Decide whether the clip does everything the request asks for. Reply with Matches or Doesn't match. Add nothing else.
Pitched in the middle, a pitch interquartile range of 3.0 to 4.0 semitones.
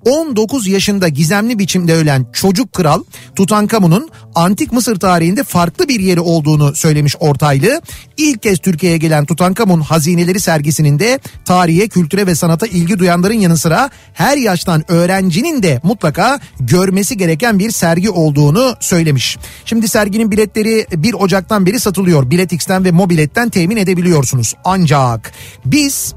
Doesn't match